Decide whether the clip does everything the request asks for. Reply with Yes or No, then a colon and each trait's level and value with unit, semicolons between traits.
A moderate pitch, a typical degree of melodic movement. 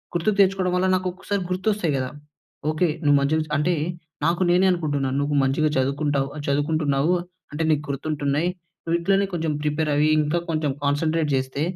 Yes: medium, 155 Hz; average, 3.5 semitones